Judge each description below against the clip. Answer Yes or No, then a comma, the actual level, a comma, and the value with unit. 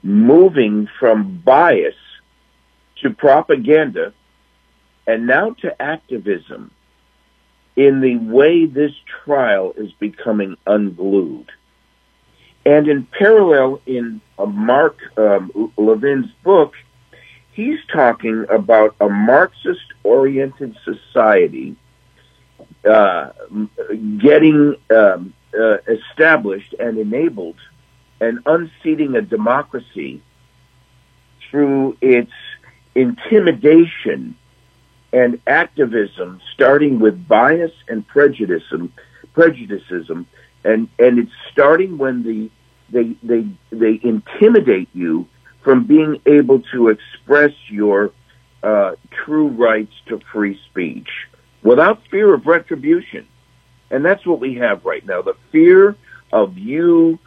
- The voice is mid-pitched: No, low, 130 Hz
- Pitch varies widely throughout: Yes, wide, 7.5 semitones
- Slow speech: Yes, slow, 95 wpm